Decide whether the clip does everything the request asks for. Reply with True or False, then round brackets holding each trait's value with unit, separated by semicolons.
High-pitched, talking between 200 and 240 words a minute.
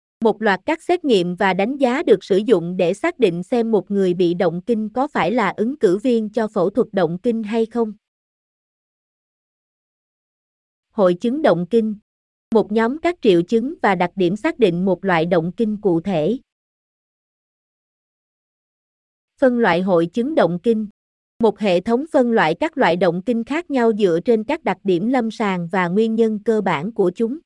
False (220 Hz; 185 wpm)